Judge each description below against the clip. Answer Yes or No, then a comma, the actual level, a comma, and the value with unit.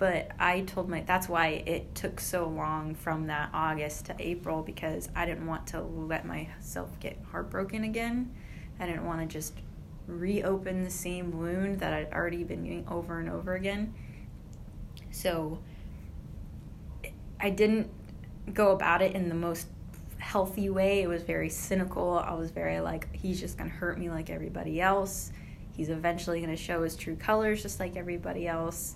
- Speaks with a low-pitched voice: No, medium, 170 Hz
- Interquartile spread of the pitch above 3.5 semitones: No, average, 3.1 semitones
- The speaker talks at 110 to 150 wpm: No, average, 170 wpm